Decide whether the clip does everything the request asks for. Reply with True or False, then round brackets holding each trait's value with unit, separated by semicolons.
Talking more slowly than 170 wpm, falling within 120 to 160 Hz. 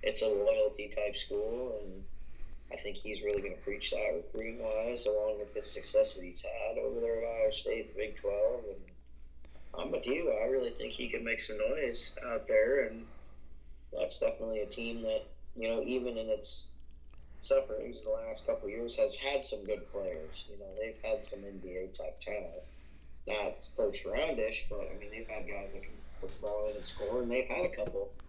False (200 wpm; 140 Hz)